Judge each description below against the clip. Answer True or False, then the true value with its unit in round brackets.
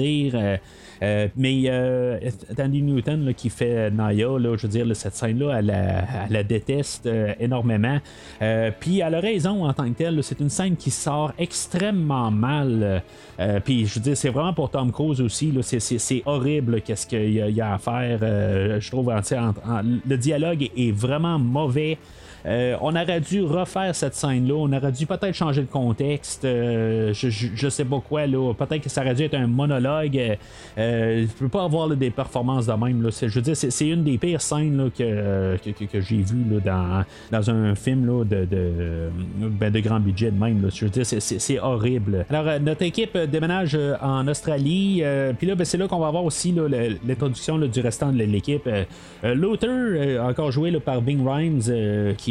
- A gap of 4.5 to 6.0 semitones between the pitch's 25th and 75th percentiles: True (5.0 semitones)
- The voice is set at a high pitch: False (125 Hz)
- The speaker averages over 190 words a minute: True (215 wpm)